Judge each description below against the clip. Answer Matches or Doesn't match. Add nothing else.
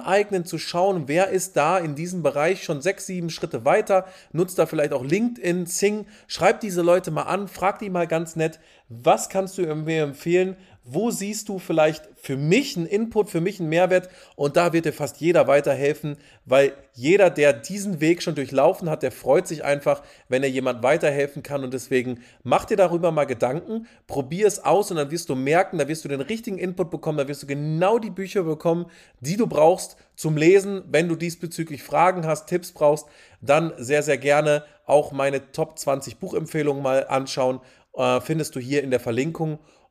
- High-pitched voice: Doesn't match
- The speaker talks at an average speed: Doesn't match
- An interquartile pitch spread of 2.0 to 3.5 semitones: Doesn't match